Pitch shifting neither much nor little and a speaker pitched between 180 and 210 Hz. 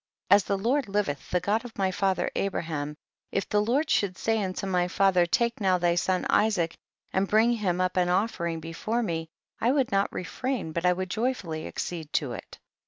Yes: average, 3.7 semitones; high, 190 Hz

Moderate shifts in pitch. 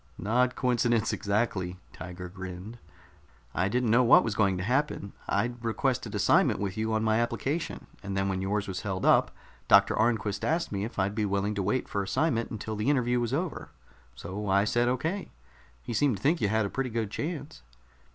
Yes: average, 3.8 semitones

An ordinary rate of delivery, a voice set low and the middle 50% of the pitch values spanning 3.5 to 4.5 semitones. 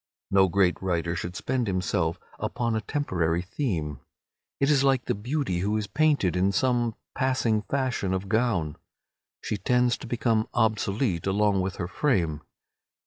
No: average, 150 wpm; low, 105 Hz; average, 5.2 semitones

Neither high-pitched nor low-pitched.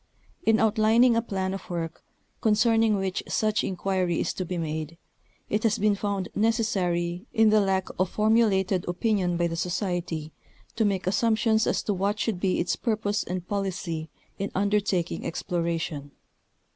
No: high, 195 Hz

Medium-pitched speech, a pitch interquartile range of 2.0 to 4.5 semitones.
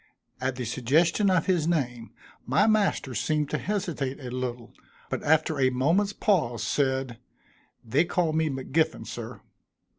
No: medium, 145 Hz; average, 4.9 semitones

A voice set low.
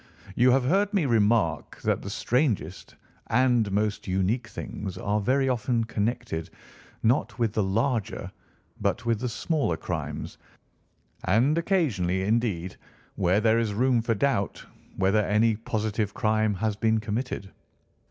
Yes: low, 110 Hz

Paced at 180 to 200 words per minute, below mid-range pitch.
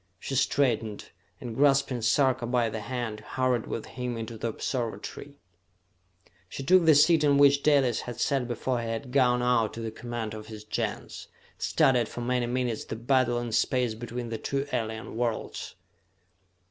No: average, 170 wpm; low, 120 Hz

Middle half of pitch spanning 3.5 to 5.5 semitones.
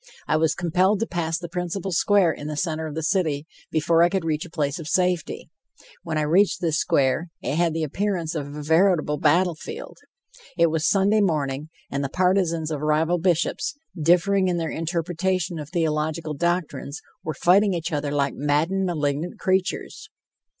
No: average, 3.0 semitones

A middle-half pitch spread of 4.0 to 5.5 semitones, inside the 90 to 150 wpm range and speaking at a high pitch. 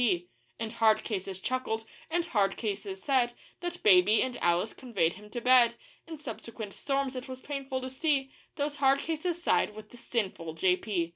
No: average, 5.2 semitones; average, 180 wpm; high, 235 Hz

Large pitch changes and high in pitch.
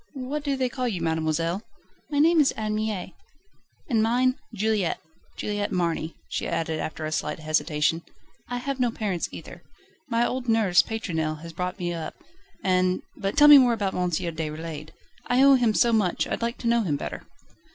Yes: wide, 6.6 semitones; high, 205 Hz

